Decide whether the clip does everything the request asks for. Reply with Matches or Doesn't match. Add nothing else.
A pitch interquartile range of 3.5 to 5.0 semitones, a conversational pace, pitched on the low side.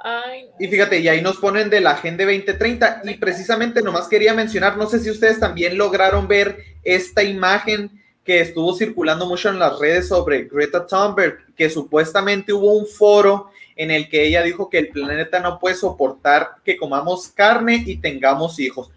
Doesn't match